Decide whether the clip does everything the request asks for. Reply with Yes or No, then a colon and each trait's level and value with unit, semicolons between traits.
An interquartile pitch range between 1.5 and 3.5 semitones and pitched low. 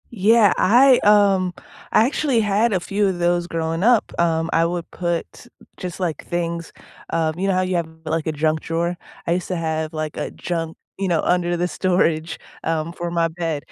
No: narrow, 2.5 semitones; medium, 175 Hz